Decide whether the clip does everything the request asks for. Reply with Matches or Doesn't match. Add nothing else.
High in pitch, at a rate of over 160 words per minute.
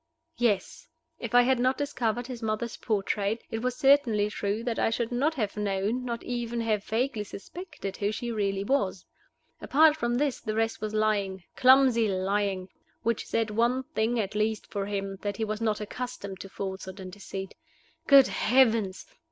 Matches